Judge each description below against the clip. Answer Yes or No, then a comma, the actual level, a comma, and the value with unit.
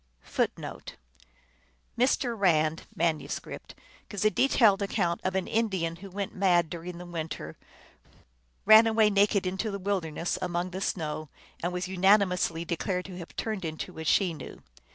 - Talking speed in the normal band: Yes, average, 155 wpm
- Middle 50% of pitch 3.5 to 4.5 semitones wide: No, average, 2.9 semitones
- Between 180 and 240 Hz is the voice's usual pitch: Yes, medium, 185 Hz